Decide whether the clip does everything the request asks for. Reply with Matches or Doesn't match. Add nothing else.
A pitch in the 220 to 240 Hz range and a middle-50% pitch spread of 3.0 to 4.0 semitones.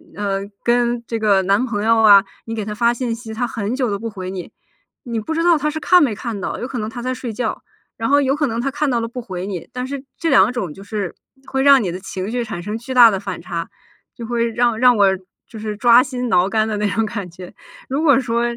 Matches